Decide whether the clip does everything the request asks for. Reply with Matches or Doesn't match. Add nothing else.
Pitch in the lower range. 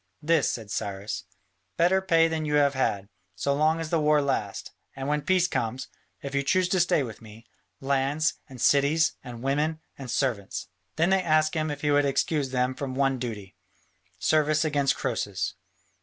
Doesn't match